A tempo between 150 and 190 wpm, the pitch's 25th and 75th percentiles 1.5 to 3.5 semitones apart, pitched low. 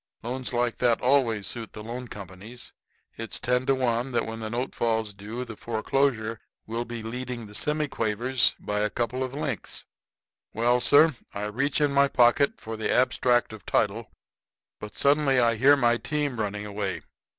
Yes: average, 175 wpm; average, 2.8 semitones; low, 120 Hz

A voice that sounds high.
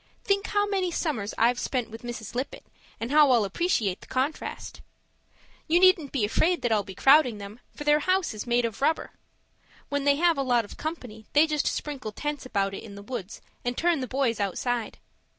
Yes: very high, 255 Hz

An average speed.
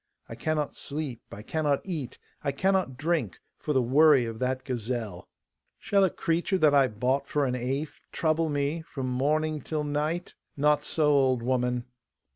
Yes: average, 165 wpm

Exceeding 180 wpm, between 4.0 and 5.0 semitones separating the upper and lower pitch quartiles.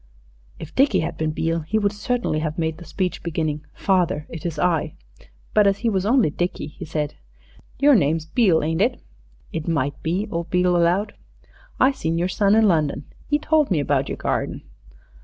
Yes: average, 190 wpm; average, 4.5 semitones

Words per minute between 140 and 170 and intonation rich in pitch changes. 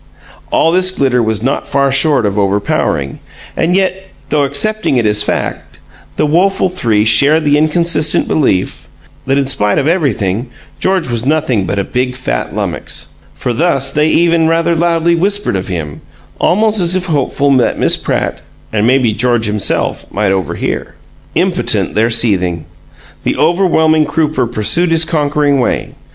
Yes: average, 155 wpm; wide, 7.1 semitones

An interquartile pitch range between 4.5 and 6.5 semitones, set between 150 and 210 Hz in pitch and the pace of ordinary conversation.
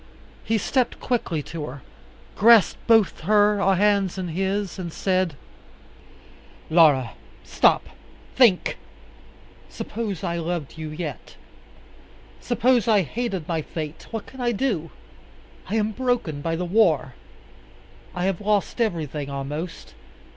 No: average, 5.3 semitones; medium, 185 Hz; slow, 120 wpm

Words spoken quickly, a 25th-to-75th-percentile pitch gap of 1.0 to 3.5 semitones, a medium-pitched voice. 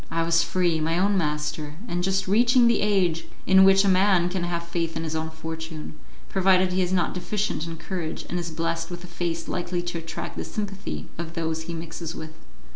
Yes: fast, 210 wpm; narrow, 2.5 semitones; medium, 175 Hz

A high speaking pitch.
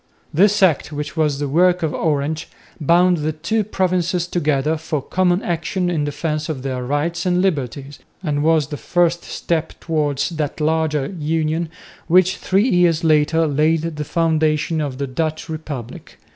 No: medium, 160 Hz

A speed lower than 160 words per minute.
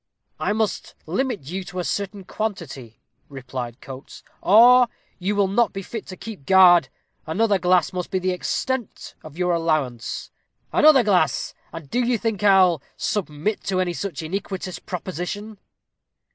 Yes: average, 150 wpm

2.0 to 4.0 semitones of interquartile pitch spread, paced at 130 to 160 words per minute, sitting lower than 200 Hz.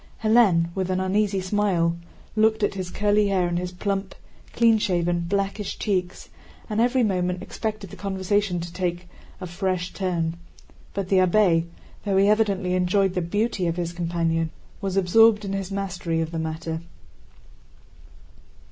Yes: average, 2.7 semitones; average, 155 wpm; medium, 185 Hz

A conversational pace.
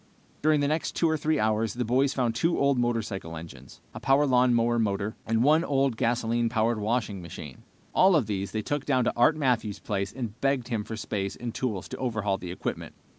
No: fast, 215 wpm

